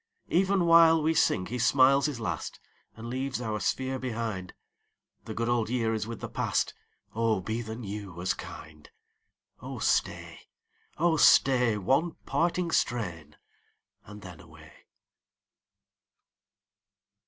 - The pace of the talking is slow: Yes, slow, 130 wpm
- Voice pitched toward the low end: Yes, low, 115 Hz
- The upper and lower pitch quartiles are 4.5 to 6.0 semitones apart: Yes, average, 4.8 semitones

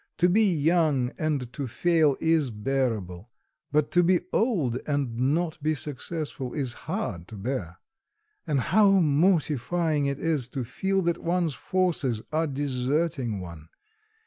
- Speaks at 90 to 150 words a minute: Yes, average, 140 wpm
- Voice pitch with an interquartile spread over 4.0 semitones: Yes, average, 5.1 semitones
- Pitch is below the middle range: No, medium, 145 Hz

